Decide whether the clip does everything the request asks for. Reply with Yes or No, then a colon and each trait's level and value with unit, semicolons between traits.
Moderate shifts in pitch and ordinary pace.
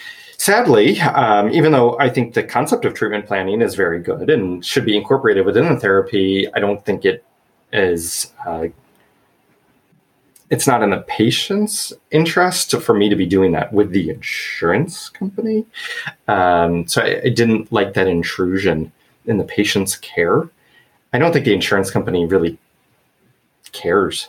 No: wide, 7.1 semitones; average, 155 wpm